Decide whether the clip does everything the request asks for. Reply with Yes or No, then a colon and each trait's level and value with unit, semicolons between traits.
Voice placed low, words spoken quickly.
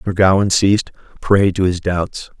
No: very low, 95 Hz; average, 175 wpm